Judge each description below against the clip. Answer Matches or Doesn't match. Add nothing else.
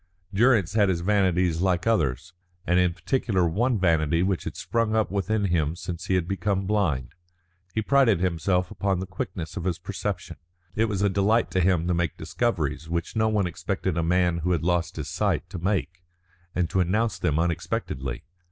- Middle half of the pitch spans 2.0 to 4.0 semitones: Matches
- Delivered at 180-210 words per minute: Matches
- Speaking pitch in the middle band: Doesn't match